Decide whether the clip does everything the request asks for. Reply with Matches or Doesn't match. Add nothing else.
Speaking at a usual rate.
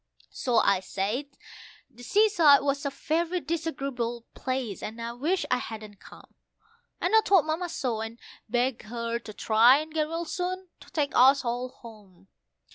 Matches